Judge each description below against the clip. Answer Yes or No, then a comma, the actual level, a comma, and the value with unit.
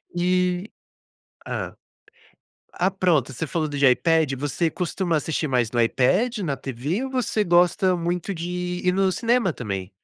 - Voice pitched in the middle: Yes, medium, 175 Hz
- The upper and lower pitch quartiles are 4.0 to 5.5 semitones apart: Yes, average, 4.5 semitones